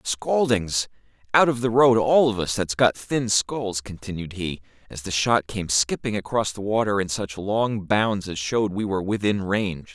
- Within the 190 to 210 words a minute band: Yes, average, 195 wpm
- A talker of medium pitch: No, low, 105 Hz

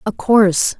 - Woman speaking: Yes, female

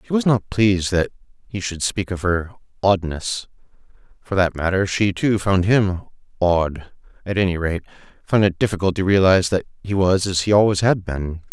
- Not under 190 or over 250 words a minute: No, average, 175 wpm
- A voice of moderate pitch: No, very low, 95 Hz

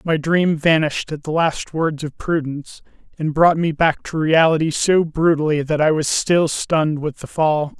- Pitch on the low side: No, medium, 155 Hz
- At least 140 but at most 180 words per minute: No, average, 190 wpm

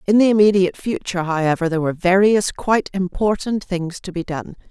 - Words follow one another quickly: No, average, 180 wpm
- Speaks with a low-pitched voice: No, medium, 185 Hz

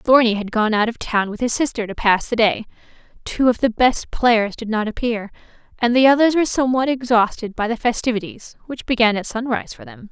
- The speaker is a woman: Yes, female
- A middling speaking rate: No, fast, 215 wpm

